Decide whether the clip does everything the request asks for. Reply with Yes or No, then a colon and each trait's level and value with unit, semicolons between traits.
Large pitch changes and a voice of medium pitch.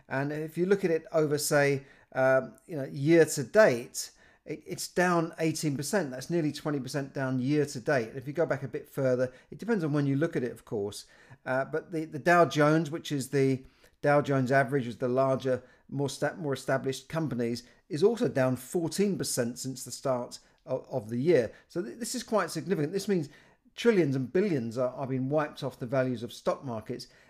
No: average, 3.7 semitones; medium, 145 Hz